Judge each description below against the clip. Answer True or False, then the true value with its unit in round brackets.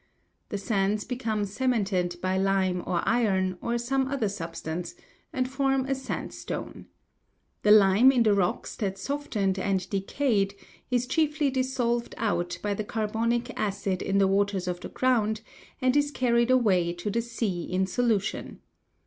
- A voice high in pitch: True (210 Hz)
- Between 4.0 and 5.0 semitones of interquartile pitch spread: True (4.5 semitones)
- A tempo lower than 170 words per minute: True (150 wpm)